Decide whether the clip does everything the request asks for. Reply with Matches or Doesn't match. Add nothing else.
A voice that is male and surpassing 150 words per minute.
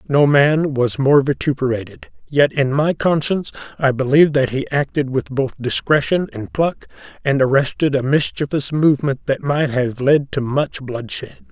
Matches